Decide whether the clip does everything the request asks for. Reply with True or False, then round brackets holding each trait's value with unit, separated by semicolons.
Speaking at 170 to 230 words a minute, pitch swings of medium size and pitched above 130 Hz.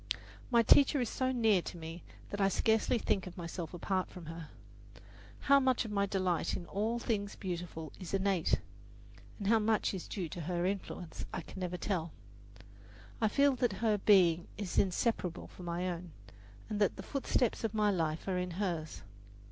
True (180 wpm; 3.8 semitones; 190 Hz)